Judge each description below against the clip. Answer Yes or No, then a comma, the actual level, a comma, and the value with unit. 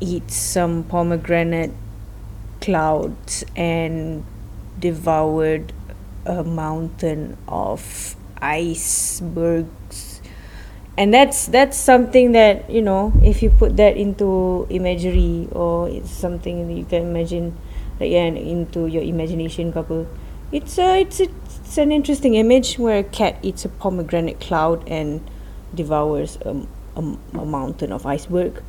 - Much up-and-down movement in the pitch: No, average, 3.7 semitones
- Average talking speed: No, slow, 125 wpm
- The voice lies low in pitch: No, medium, 170 Hz